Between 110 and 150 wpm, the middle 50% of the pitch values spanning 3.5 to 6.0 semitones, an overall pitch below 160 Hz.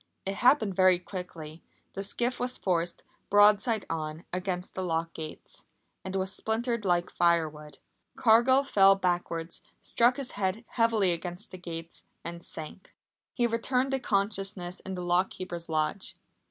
No: average, 145 wpm; average, 4.3 semitones; high, 190 Hz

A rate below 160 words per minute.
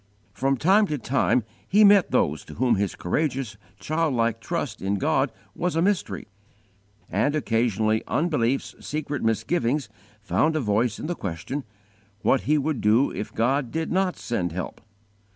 Yes: average, 150 wpm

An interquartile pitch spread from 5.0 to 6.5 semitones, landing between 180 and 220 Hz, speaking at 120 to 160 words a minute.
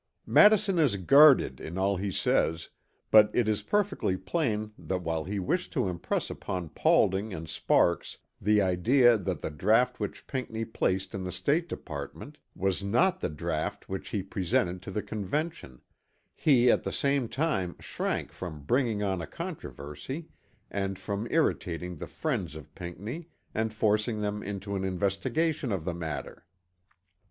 No: average, 5.3 semitones; low, 100 Hz; average, 155 wpm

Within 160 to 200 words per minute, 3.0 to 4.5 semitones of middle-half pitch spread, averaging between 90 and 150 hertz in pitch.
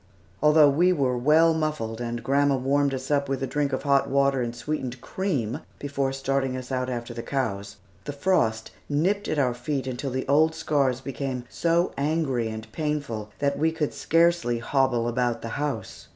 Yes: average, 180 wpm; average, 3.4 semitones; low, 135 Hz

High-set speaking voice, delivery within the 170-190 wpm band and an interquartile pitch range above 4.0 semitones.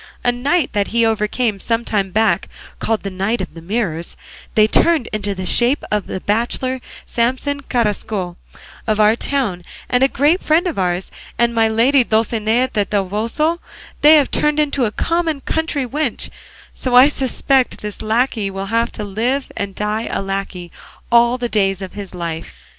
Yes: high, 225 Hz; average, 175 wpm; average, 4.4 semitones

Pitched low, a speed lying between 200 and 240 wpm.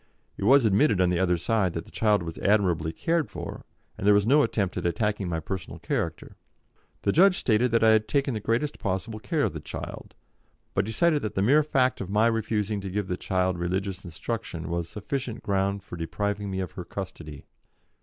Yes: low, 100 Hz; fast, 205 wpm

